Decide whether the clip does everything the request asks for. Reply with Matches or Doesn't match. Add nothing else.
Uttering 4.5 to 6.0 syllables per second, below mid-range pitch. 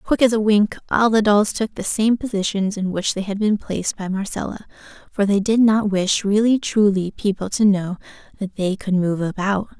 Doesn't match